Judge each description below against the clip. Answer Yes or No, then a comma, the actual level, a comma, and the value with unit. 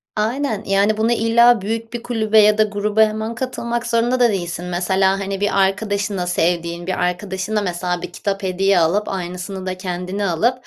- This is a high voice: Yes, high, 200 Hz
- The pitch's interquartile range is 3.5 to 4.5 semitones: No, average, 3.1 semitones